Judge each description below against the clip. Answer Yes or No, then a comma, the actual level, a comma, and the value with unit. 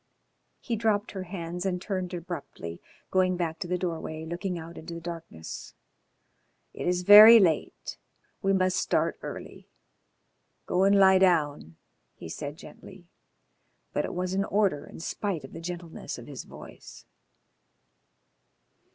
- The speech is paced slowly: No, average, 145 wpm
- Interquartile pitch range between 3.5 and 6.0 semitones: No, narrow, 2.6 semitones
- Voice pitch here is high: No, medium, 180 Hz